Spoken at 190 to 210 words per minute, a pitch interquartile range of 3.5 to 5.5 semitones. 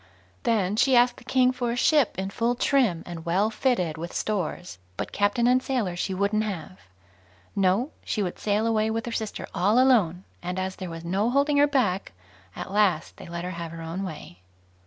Yes: average, 200 wpm; average, 5.1 semitones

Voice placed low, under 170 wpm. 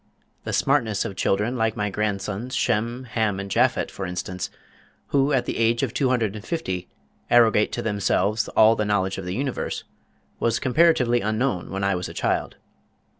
No: low, 110 Hz; average, 175 wpm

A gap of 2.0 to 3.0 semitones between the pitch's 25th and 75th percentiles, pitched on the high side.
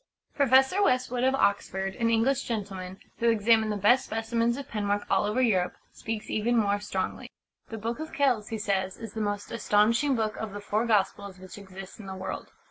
Yes: average, 2.7 semitones; high, 215 Hz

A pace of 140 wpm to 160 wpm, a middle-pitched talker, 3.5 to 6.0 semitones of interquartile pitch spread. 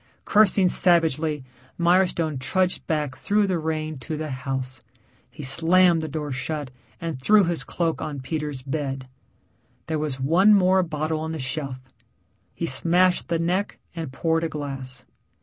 Yes: average, 150 wpm; medium, 155 Hz; average, 3.9 semitones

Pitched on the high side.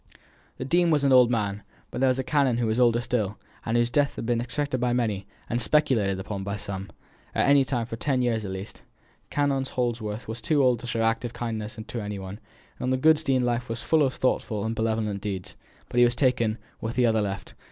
No: low, 120 Hz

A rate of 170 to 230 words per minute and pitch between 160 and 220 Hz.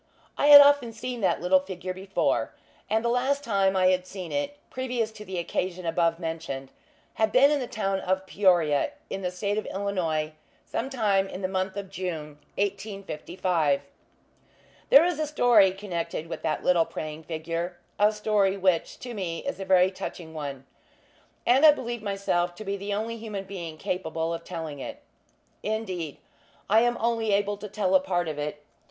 Yes: average, 180 wpm; high, 190 Hz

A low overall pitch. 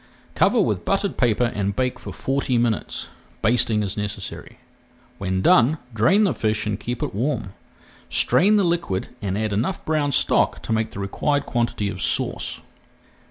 Yes: low, 115 Hz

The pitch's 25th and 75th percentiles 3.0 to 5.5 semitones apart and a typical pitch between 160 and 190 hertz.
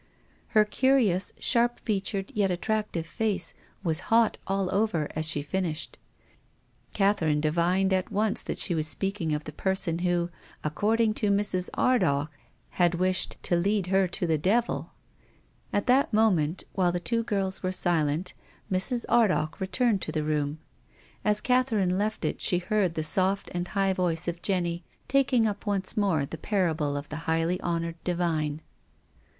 Yes: average, 3.9 semitones; medium, 185 Hz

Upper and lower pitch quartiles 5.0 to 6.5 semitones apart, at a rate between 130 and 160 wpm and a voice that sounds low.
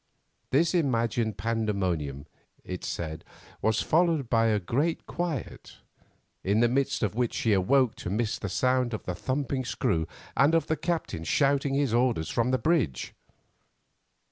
Yes: wide, 5.6 semitones; average, 150 wpm; low, 120 Hz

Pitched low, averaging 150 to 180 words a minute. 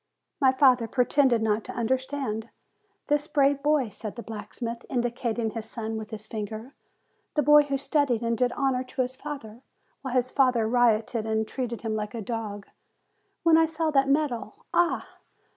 No: high, 245 Hz; average, 170 wpm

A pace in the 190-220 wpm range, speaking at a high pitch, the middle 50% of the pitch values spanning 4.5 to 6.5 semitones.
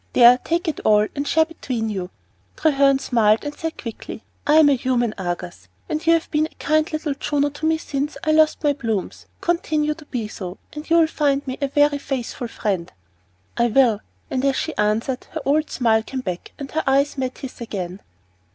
Yes: fast, 205 wpm; very high, 275 Hz; average, 5.1 semitones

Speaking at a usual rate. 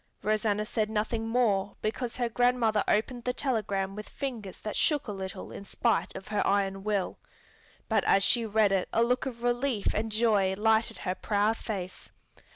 Yes: average, 175 wpm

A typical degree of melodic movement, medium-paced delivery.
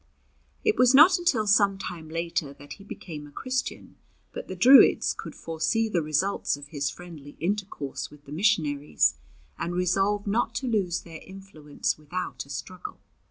No: wide, 5.7 semitones; average, 160 wpm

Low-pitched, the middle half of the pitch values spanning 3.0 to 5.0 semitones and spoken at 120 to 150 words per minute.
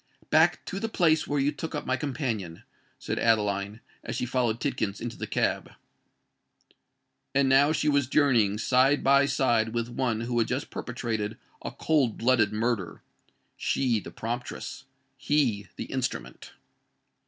Yes: low, 125 Hz; average, 3.8 semitones; average, 140 wpm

